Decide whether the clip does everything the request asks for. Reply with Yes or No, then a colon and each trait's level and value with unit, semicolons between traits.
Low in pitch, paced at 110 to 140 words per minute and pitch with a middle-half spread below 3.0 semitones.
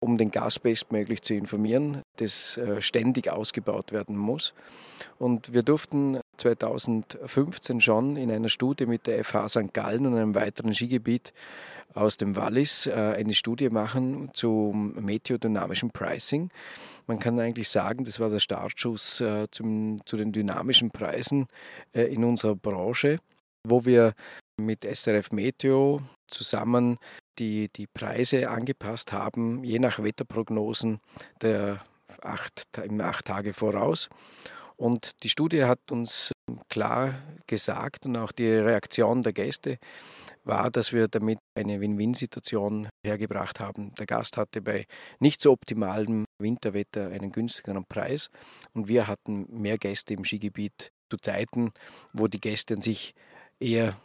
Yes: low, 110 Hz; average, 130 wpm; narrow, 2.5 semitones